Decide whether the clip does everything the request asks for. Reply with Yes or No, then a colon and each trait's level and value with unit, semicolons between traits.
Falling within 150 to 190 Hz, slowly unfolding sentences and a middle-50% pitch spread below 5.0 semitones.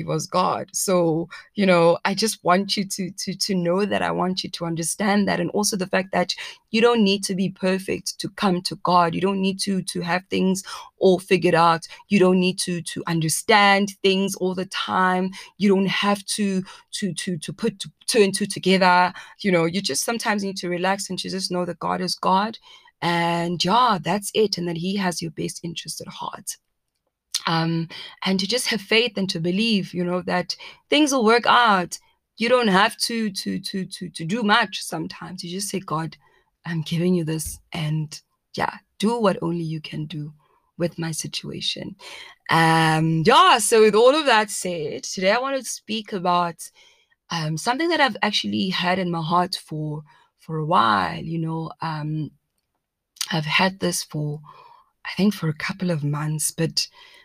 No: medium, 185 Hz; average, 195 wpm; average, 3.3 semitones